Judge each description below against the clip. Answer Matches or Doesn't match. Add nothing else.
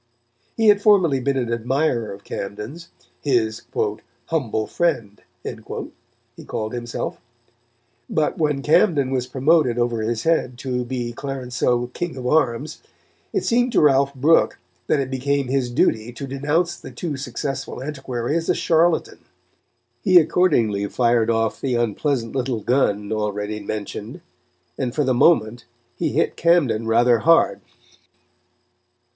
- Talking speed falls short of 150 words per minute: Matches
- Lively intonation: Doesn't match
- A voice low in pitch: Matches